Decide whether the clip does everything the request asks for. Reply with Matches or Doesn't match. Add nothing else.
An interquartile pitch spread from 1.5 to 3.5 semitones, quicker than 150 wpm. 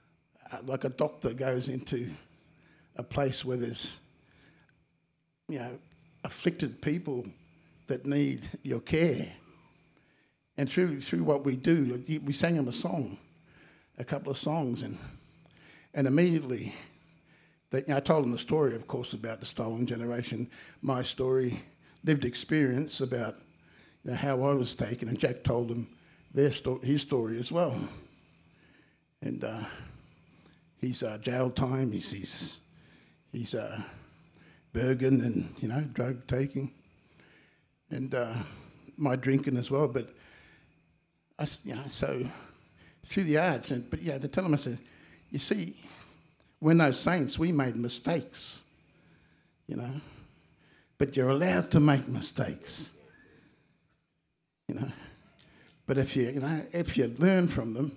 Doesn't match